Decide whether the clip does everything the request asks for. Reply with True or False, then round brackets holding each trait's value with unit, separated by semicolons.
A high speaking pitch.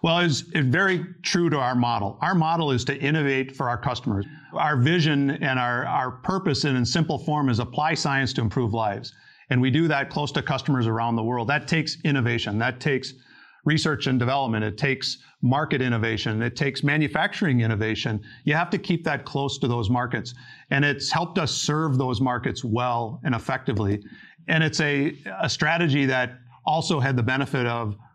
False (135 Hz)